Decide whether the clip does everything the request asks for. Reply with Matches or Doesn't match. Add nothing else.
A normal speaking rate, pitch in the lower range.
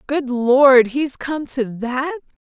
Doesn't match